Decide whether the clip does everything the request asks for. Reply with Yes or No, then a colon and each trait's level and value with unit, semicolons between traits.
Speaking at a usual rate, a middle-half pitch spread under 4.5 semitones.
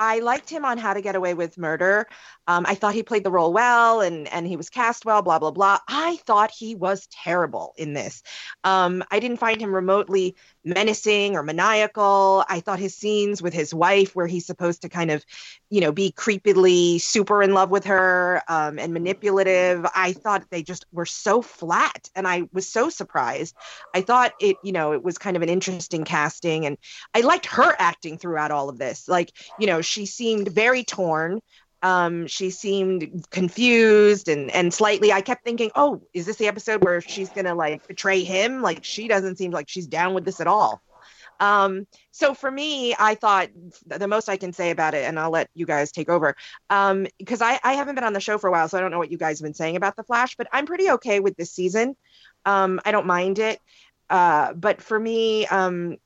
No: fast, 215 wpm; average, 3.5 semitones